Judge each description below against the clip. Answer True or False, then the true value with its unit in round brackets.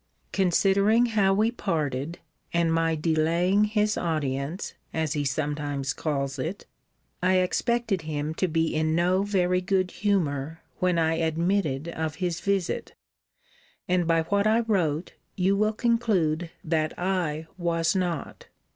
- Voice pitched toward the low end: False (170 Hz)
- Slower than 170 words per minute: True (135 wpm)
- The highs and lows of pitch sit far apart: False (3.6 semitones)